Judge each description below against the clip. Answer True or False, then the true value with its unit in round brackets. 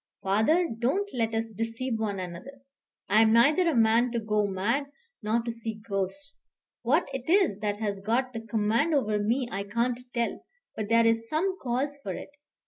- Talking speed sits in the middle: True (185 wpm)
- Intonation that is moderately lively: True (3.6 semitones)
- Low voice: False (230 Hz)